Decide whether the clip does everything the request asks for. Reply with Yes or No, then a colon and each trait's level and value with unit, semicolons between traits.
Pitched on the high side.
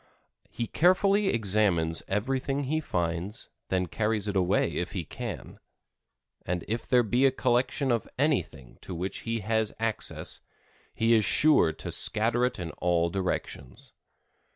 No: low, 110 Hz